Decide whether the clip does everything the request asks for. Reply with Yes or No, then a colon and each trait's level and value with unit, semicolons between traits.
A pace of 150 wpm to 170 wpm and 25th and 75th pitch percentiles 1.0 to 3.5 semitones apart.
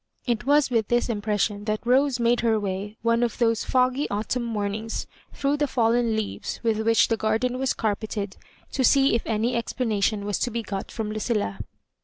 No: average, 180 wpm; narrow, 2.4 semitones